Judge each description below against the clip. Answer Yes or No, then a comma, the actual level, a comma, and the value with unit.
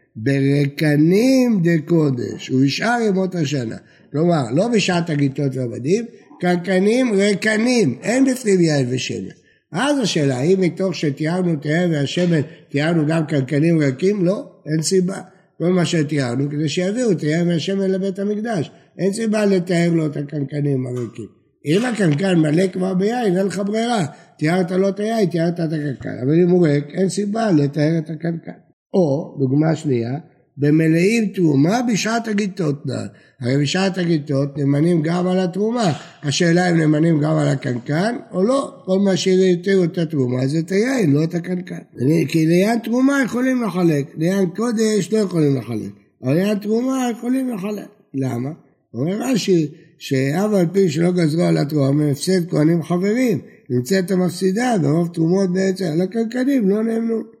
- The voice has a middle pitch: Yes, medium, 175 Hz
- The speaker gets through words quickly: Yes, fast, 155 wpm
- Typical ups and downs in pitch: Yes, average, 4.8 semitones